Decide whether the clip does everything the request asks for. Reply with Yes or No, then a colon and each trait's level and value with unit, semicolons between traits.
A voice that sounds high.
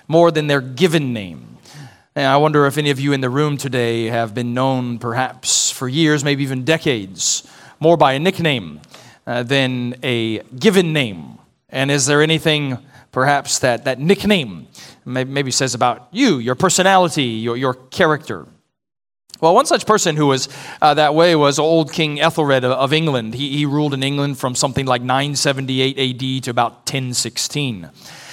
No: medium, 140 Hz